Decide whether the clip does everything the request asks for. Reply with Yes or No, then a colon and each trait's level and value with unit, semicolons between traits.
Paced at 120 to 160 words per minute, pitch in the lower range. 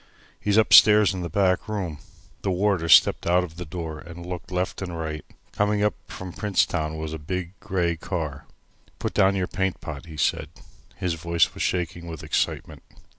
No: average, 180 wpm; very low, 90 Hz